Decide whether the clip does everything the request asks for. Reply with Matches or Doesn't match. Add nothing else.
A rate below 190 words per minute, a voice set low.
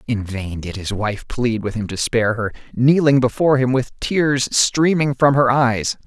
Doesn't match